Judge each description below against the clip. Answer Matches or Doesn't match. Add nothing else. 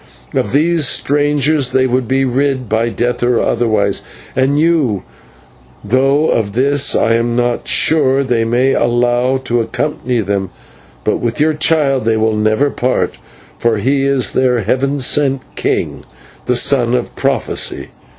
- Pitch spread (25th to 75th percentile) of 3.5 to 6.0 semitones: Doesn't match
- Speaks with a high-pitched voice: Doesn't match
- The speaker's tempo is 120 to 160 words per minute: Matches